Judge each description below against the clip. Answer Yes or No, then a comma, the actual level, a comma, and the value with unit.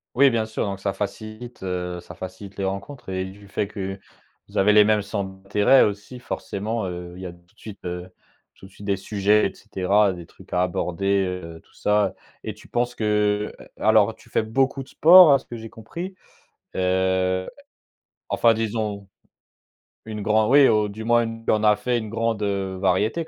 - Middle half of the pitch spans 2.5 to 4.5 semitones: Yes, average, 2.8 semitones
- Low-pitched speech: Yes, low, 105 Hz